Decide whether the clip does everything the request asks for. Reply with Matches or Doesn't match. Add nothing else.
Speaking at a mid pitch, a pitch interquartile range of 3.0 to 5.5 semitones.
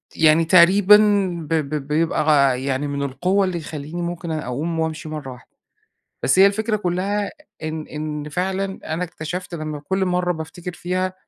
Matches